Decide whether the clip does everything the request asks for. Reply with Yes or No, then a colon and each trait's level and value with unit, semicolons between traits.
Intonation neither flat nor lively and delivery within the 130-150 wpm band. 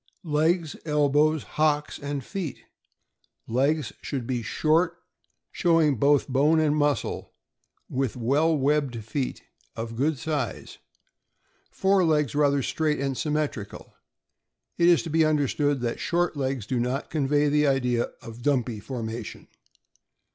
Yes: average, 3.2 semitones; slow, 135 wpm